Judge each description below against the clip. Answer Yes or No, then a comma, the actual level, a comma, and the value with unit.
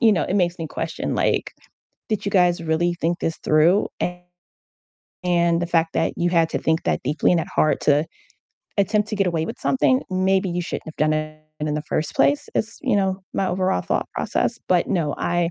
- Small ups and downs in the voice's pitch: No, average, 3.0 semitones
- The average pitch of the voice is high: No, medium, 175 Hz